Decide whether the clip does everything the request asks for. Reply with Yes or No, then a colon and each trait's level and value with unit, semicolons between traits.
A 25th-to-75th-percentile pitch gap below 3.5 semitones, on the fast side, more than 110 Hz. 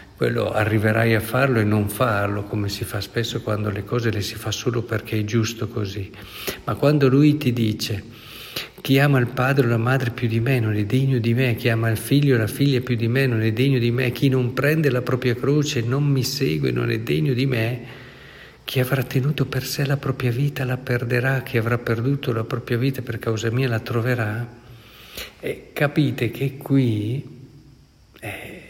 Yes: average, 2.9 semitones; fast, 205 wpm; low, 120 Hz